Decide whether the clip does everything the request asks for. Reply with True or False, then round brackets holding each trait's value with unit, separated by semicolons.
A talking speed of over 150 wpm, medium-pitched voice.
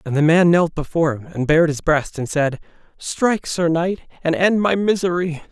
True (205 wpm; 165 Hz)